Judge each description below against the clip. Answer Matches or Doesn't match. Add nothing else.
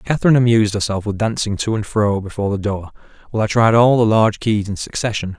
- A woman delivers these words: Doesn't match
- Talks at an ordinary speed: Doesn't match